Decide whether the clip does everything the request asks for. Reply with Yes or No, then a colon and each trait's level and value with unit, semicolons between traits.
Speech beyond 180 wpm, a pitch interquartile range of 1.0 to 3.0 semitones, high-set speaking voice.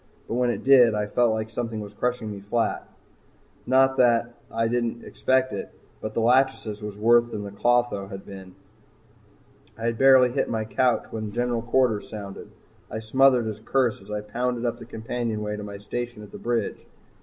No: average, 190 wpm; narrow, 2.5 semitones; low, 115 Hz